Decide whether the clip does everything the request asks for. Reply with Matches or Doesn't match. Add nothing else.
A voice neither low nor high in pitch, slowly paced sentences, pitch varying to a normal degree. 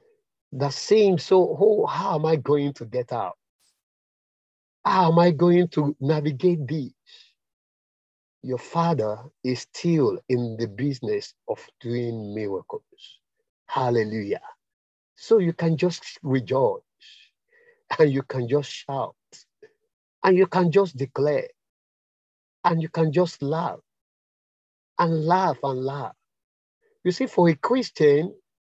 Doesn't match